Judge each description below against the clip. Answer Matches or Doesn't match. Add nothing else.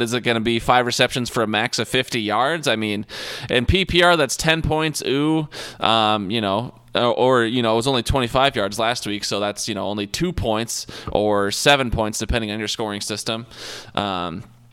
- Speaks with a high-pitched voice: Doesn't match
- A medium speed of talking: Doesn't match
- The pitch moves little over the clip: Doesn't match